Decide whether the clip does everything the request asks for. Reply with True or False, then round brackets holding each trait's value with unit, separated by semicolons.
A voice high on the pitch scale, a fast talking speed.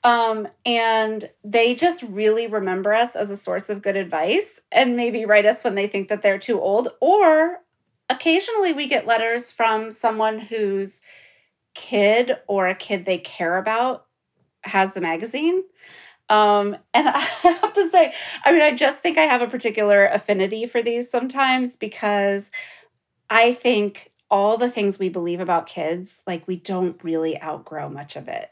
False (220 Hz; 165 wpm)